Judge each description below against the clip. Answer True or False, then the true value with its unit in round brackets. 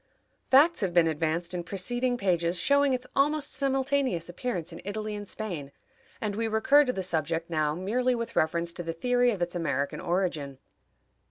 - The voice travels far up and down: True (6.6 semitones)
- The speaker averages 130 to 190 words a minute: True (175 wpm)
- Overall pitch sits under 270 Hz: True (190 Hz)